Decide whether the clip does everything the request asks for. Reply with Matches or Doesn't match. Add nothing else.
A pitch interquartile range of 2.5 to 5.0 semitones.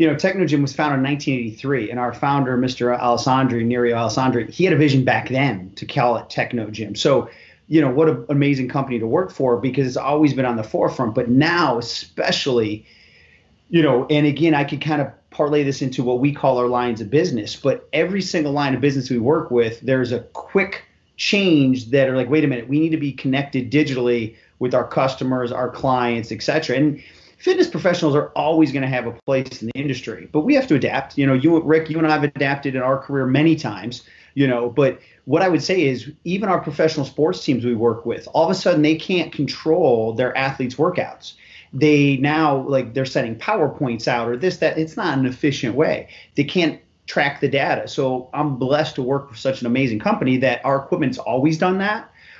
Matches